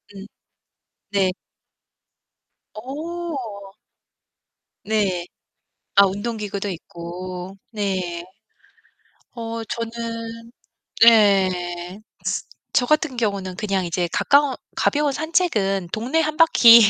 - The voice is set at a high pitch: Yes, high, 210 Hz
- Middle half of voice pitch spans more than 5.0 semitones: No, average, 4.3 semitones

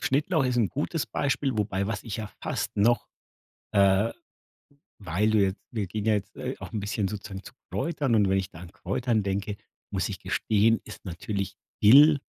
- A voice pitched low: Yes, low, 105 Hz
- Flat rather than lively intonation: No, average, 3.7 semitones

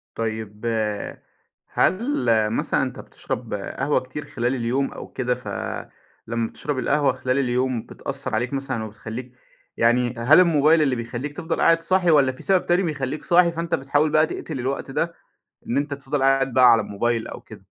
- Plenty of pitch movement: No, average, 3.8 semitones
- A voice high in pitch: No, low, 135 Hz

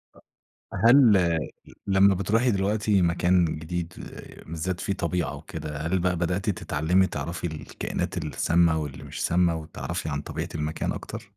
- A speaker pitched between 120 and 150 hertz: No, very low, 85 Hz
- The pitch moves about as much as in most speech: Yes, average, 3.3 semitones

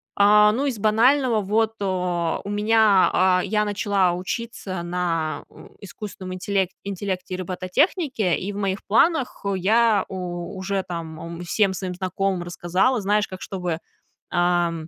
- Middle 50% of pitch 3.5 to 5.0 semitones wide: No, average, 2.9 semitones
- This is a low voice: No, high, 190 Hz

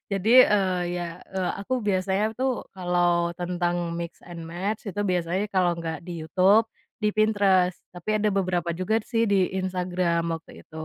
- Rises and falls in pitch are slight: Yes, narrow, 2.2 semitones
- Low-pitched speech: No, medium, 180 Hz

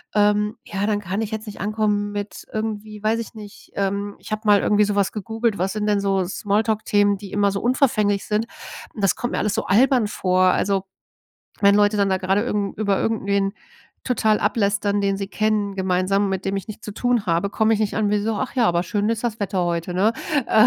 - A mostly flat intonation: Yes, narrow, 1.5 semitones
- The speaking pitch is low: No, high, 205 Hz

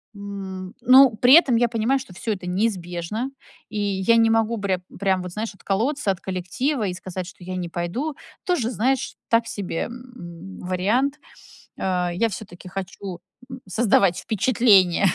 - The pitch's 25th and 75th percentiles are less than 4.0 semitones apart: No, average, 4.3 semitones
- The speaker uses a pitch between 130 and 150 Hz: No, high, 200 Hz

